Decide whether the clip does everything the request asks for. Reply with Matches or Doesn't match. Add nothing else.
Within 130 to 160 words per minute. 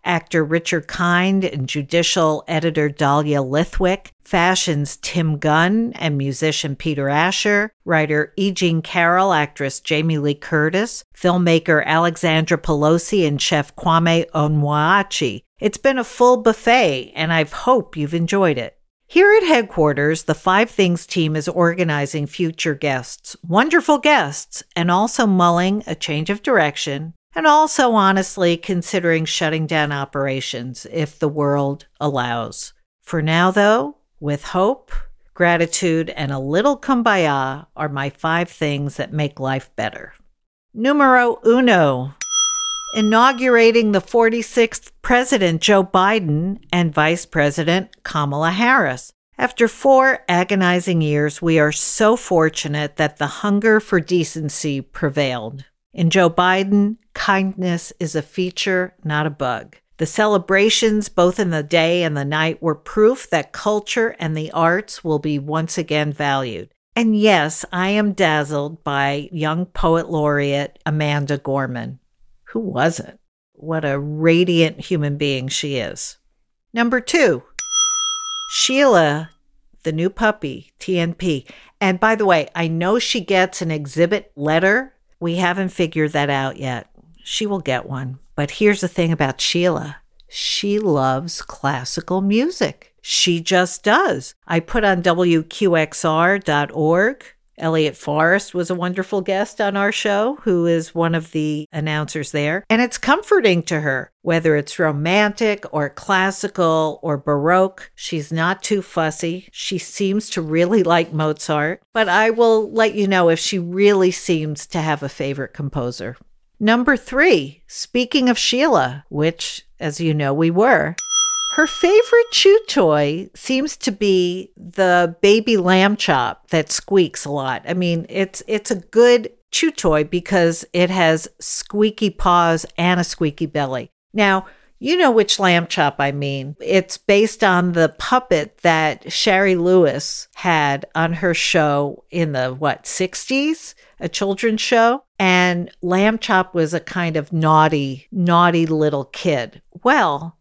Matches